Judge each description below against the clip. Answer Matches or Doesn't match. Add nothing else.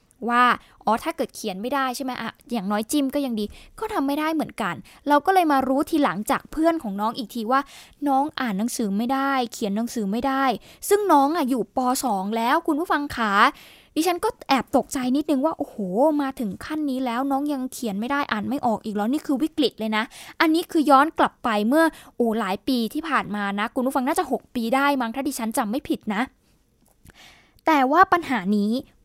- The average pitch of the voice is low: Doesn't match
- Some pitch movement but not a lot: Matches